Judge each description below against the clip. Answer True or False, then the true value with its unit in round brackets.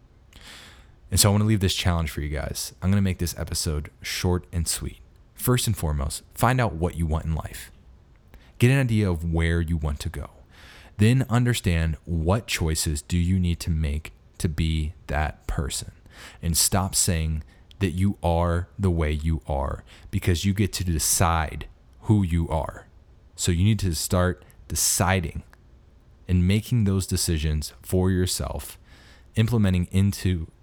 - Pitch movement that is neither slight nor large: True (3.5 semitones)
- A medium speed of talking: True (165 wpm)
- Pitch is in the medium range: False (85 Hz)